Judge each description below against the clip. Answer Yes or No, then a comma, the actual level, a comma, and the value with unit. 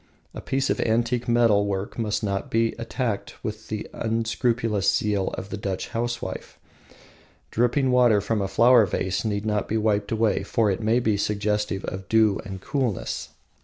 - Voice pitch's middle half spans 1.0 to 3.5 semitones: Yes, narrow, 2.4 semitones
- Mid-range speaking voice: No, low, 110 Hz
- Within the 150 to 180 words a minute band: Yes, average, 165 wpm